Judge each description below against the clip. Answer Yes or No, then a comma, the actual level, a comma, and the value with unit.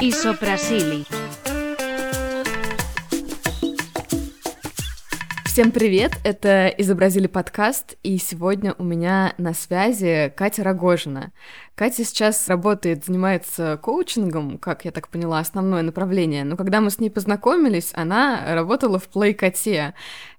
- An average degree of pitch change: Yes, average, 4.6 semitones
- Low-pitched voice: No, high, 190 Hz